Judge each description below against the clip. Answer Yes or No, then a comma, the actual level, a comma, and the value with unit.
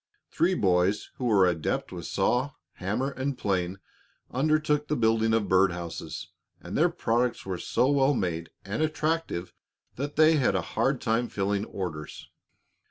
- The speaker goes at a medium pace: Yes, average, 155 wpm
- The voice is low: Yes, low, 115 Hz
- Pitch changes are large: Yes, wide, 7.0 semitones